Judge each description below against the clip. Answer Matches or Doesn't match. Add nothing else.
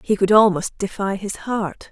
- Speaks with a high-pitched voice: Matches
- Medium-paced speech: Matches